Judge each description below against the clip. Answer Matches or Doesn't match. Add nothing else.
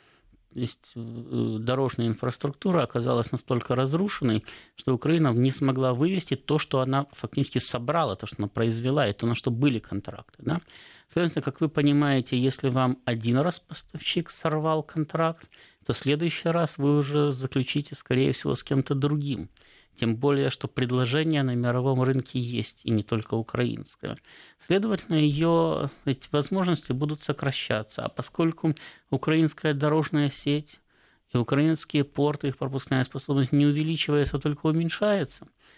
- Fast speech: Doesn't match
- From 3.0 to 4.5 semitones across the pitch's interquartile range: Matches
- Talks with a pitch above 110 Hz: Matches